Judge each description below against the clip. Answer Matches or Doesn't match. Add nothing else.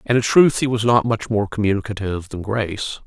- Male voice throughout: Matches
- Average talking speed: Doesn't match